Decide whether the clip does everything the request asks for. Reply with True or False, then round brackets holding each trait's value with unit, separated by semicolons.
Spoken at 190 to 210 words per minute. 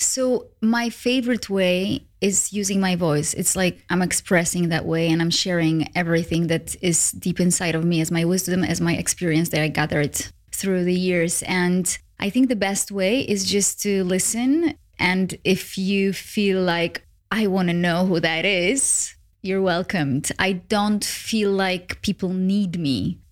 False (170 wpm)